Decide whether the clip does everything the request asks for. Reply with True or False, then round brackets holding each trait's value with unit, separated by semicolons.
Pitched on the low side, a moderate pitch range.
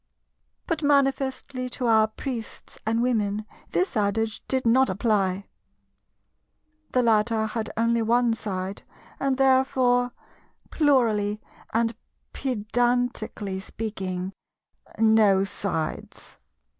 False (225 Hz; 3.3 semitones)